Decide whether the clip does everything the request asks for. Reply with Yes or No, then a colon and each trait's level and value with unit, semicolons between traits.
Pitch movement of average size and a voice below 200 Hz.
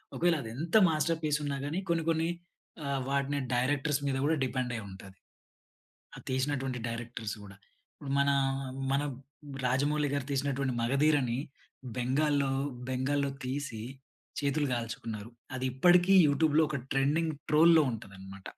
Yes: average, 3.1 semitones; medium, 140 Hz